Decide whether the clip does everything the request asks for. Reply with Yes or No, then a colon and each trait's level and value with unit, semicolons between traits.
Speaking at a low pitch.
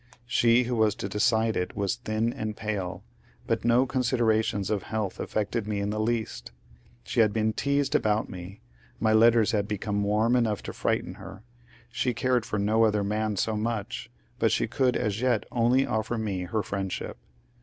Yes: low, 110 Hz